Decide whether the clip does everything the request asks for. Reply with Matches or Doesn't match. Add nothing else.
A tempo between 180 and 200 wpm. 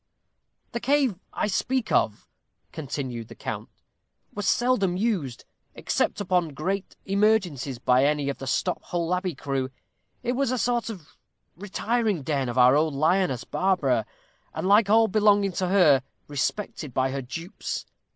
Doesn't match